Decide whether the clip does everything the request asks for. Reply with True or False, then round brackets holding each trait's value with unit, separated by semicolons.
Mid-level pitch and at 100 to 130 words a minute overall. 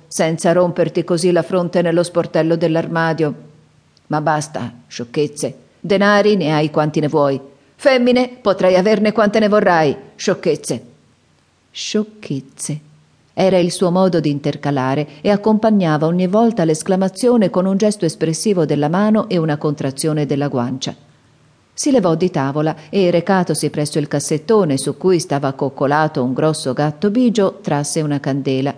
False (160 Hz; 140 wpm)